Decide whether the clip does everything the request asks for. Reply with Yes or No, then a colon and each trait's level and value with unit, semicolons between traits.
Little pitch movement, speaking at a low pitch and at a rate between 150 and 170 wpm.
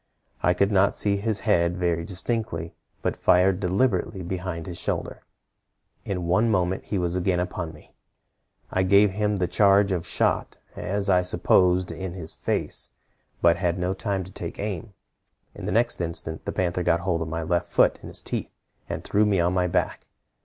No: narrow, 2.2 semitones; very low, 90 Hz; average, 185 wpm